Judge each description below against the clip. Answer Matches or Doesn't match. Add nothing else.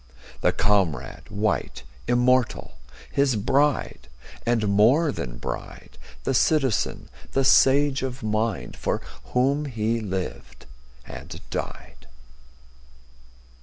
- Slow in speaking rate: Matches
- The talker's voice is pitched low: Matches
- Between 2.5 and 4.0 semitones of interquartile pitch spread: Doesn't match